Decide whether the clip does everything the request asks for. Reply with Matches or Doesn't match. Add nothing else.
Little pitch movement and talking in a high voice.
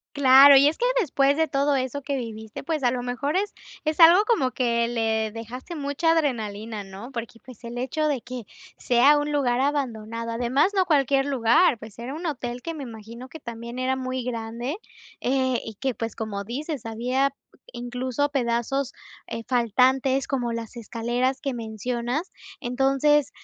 Doesn't match